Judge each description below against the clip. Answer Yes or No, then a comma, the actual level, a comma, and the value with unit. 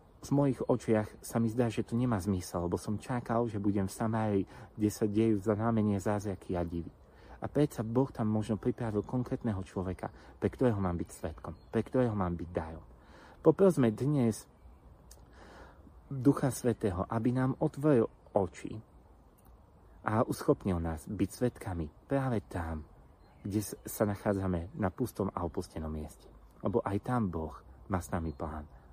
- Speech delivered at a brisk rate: No, average, 155 wpm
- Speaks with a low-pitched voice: Yes, low, 105 Hz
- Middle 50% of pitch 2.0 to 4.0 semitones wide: No, average, 5.1 semitones